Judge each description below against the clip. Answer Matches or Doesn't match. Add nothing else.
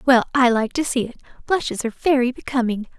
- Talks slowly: Doesn't match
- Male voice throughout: Doesn't match